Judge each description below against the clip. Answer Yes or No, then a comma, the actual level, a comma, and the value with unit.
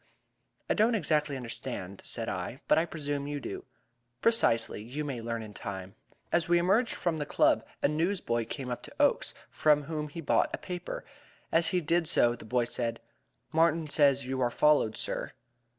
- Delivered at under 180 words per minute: No, average, 190 wpm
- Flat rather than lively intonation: No, wide, 5.5 semitones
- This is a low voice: No, medium, 145 Hz